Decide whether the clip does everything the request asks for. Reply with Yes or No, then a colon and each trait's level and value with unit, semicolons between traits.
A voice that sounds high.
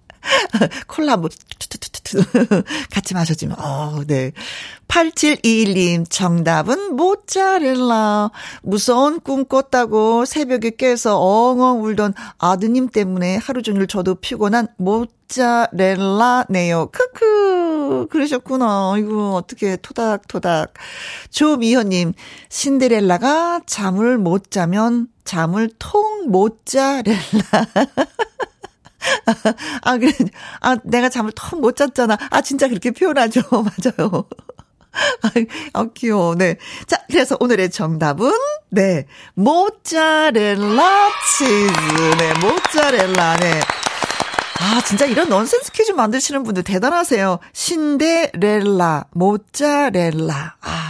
Yes: high, 230 Hz